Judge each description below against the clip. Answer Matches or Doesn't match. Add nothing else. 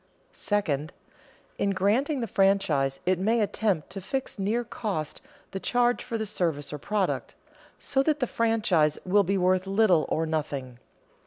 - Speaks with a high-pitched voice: Matches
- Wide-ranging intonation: Matches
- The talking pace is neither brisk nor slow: Matches